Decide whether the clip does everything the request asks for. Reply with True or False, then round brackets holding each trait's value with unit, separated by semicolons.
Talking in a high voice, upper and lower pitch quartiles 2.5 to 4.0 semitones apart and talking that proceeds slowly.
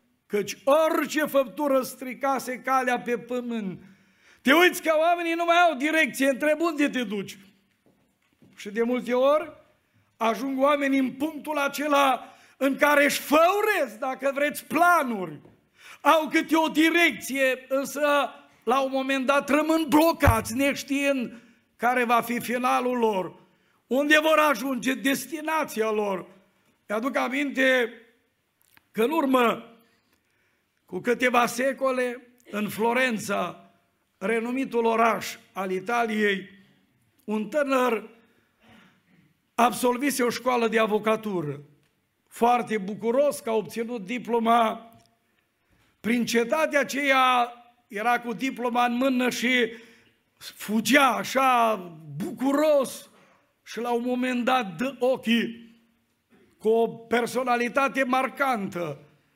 True (250 Hz; 3.5 semitones; 110 wpm)